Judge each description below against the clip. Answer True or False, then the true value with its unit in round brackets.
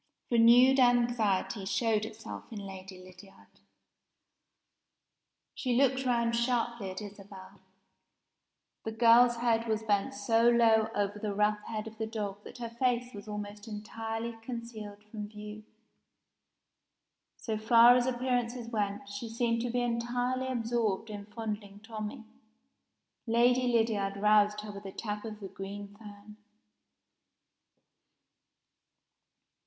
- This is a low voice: False (220 Hz)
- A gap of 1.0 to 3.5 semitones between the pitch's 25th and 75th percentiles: True (2.4 semitones)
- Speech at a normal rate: False (125 wpm)